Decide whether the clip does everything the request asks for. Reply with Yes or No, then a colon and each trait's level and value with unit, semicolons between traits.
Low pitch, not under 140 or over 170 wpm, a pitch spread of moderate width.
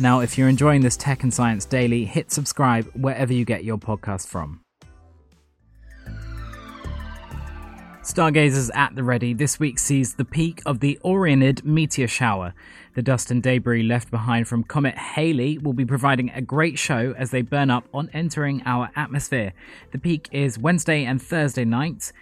Yes: low, 130 Hz; average, 165 wpm; average, 3.7 semitones